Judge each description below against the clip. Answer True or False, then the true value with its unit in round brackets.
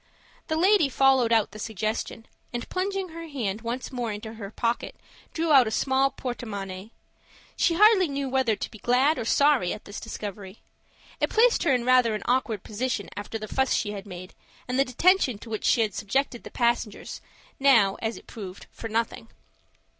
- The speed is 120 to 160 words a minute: False (190 wpm)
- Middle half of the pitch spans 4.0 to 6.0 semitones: True (4.3 semitones)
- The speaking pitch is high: True (235 Hz)